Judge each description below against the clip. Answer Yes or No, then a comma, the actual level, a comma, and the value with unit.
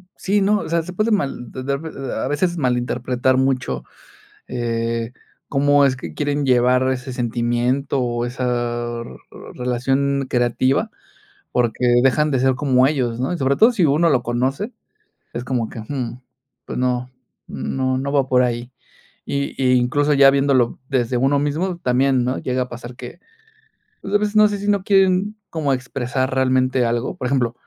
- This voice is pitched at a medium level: No, low, 130 Hz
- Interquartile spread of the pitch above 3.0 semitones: No, average, 2.7 semitones